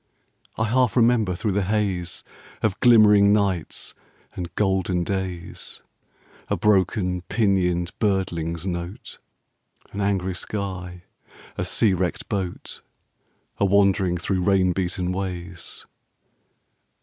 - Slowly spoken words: Yes, slow, 105 wpm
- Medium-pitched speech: No, very low, 95 Hz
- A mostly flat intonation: Yes, narrow, 2.2 semitones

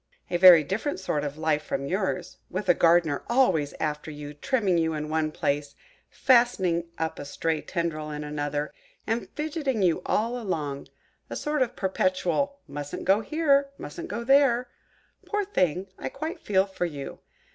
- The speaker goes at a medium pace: Yes, average, 155 wpm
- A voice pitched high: No, medium, 180 Hz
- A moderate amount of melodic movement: No, wide, 7.9 semitones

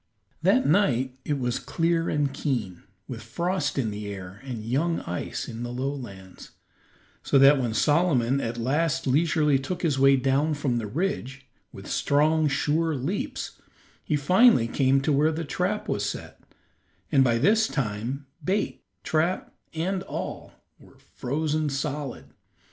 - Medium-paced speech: Yes, average, 150 wpm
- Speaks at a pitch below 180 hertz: Yes, medium, 140 Hz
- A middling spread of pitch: Yes, average, 4.5 semitones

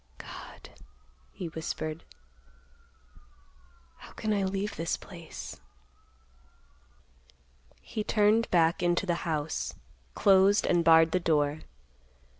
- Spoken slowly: Yes, slow, 95 wpm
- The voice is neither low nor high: Yes, medium, 175 Hz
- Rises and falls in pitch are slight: No, average, 3.3 semitones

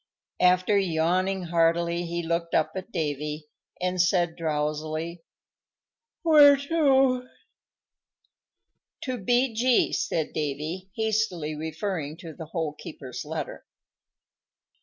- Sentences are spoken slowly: Yes, slow, 95 wpm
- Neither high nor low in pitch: Yes, medium, 170 Hz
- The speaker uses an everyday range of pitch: Yes, average, 4.4 semitones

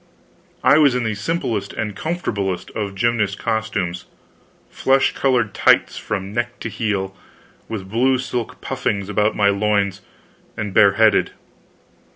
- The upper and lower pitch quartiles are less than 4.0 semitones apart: Yes, average, 3.2 semitones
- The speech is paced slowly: Yes, slow, 130 wpm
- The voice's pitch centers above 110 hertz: No, low, 105 Hz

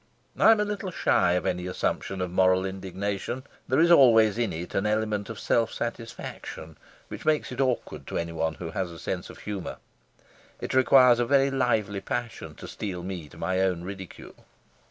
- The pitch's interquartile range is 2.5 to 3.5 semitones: No, average, 5.0 semitones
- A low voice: Yes, low, 100 Hz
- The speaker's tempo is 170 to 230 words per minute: Yes, average, 185 wpm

